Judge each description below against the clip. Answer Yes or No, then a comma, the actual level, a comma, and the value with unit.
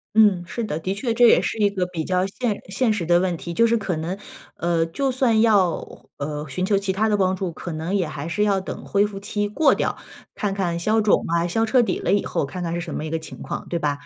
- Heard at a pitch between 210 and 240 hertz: No, high, 190 Hz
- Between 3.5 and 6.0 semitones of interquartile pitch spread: Yes, average, 3.8 semitones